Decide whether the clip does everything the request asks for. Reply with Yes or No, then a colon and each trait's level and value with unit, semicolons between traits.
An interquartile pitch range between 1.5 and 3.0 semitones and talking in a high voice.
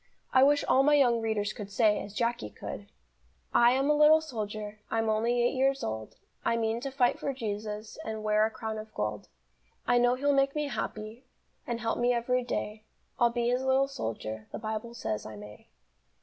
No: average, 3.4 semitones; high, 230 Hz